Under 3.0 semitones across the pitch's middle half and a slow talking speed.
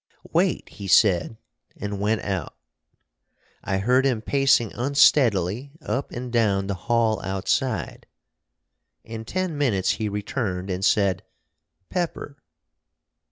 No: average, 4.8 semitones; slow, 115 wpm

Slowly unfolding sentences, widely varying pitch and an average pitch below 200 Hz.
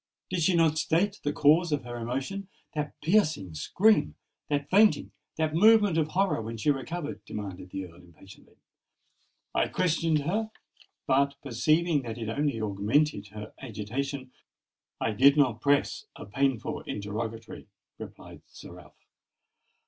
Yes: slow, 130 wpm; wide, 6.4 semitones; medium, 140 Hz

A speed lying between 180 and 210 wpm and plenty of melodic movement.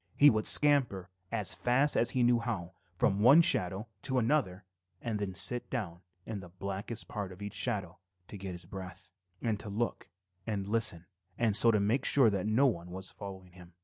No: average, 190 wpm; average, 4.1 semitones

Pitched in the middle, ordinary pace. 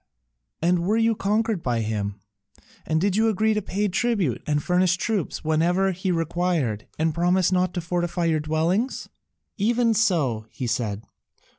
Yes: medium, 175 Hz; average, 155 wpm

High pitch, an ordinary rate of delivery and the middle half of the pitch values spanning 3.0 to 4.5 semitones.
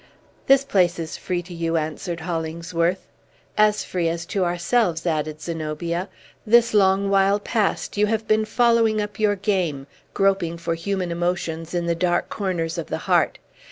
No: medium, 180 Hz; average, 160 wpm; average, 3.5 semitones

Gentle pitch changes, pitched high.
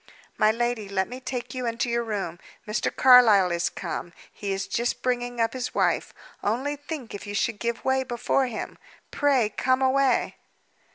No: average, 3.5 semitones; high, 240 Hz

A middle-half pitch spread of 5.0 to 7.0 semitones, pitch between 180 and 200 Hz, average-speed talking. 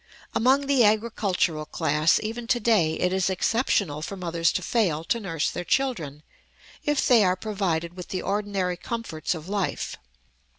Yes: average, 5.3 semitones; high, 190 Hz; average, 160 wpm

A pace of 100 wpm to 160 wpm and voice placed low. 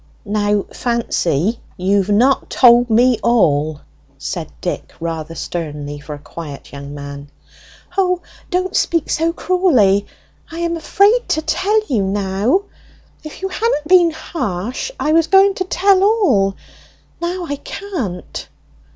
No: slow, 135 wpm; high, 240 Hz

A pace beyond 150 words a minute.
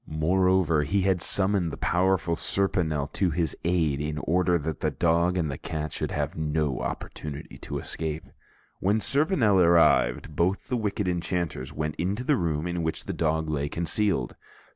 Yes: average, 165 wpm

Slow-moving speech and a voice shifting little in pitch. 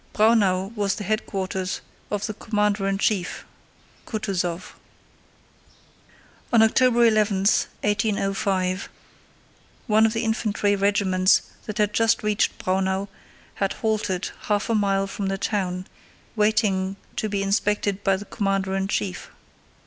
Yes: slow, 125 wpm; narrow, 1.9 semitones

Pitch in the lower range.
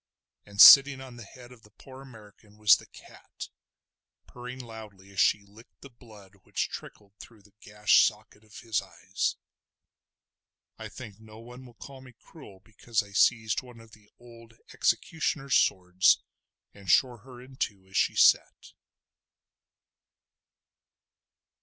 Yes: low, 110 Hz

